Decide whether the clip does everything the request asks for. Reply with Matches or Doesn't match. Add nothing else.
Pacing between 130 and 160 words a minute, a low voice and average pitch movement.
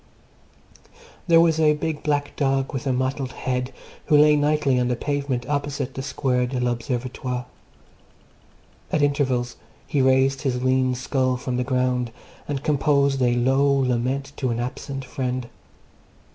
Doesn't match